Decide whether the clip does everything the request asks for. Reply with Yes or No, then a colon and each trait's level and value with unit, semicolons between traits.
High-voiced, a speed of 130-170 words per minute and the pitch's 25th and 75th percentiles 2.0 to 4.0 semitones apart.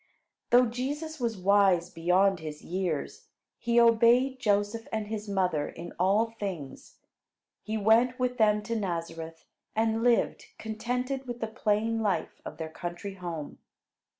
No: high, 210 Hz; average, 140 wpm; average, 4.5 semitones